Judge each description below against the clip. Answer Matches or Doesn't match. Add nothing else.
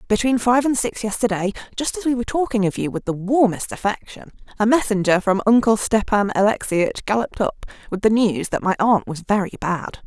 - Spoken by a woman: Matches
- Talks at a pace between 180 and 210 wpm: Matches